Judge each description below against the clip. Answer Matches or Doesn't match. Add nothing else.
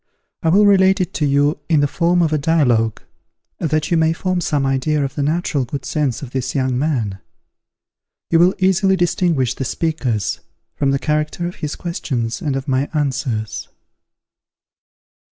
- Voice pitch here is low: Doesn't match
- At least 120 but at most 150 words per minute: Doesn't match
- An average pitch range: Matches